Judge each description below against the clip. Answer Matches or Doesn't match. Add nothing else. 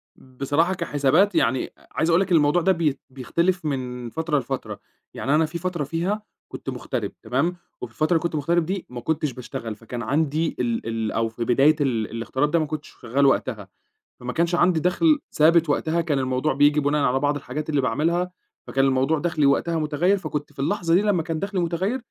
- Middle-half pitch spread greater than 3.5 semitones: Matches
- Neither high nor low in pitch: Matches